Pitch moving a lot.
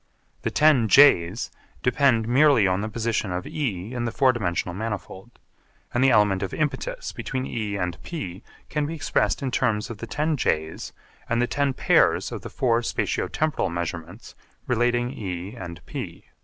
Yes: wide, 5.7 semitones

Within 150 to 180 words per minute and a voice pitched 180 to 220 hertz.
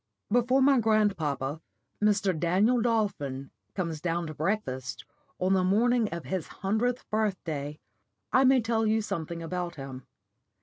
No: average, 140 wpm; high, 190 Hz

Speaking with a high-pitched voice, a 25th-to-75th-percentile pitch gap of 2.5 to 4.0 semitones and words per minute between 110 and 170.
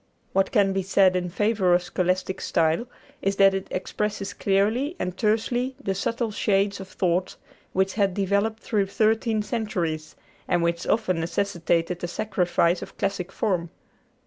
Yes: high, 195 Hz; average, 2.9 semitones; average, 150 wpm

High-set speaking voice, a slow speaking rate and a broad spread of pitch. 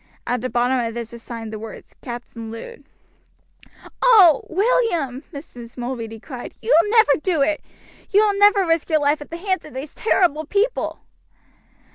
No: very high, 295 Hz; average, 170 wpm; wide, 8.1 semitones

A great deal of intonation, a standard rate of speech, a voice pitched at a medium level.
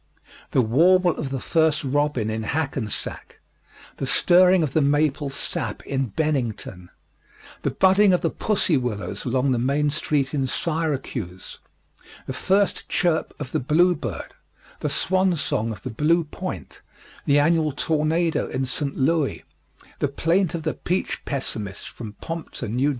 No: average, 4.2 semitones; average, 150 wpm; medium, 145 Hz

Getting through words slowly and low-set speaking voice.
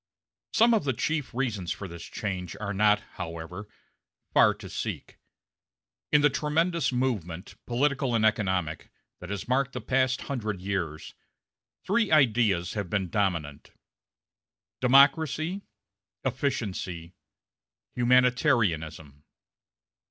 Yes: slow, 105 wpm; low, 110 Hz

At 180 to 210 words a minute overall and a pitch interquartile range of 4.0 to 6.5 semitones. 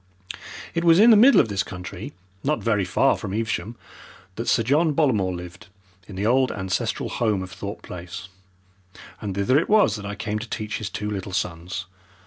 Yes: average, 190 wpm; average, 5.2 semitones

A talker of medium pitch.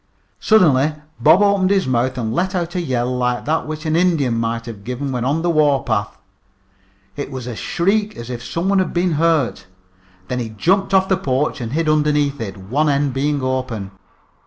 Yes: medium, 145 Hz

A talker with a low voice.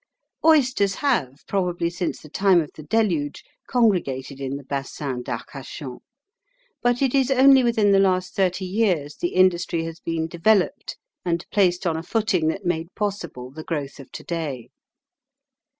No: medium, 175 Hz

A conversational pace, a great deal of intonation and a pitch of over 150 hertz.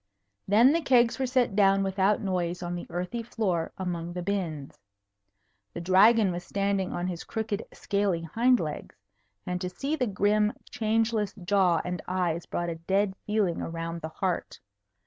No: average, 165 wpm; average, 3.5 semitones; high, 190 Hz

